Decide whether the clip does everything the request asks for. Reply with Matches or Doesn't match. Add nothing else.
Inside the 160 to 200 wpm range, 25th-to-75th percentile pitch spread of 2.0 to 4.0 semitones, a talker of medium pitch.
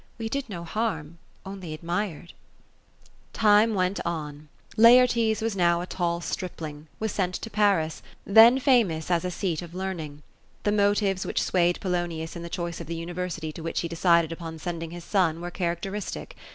Matches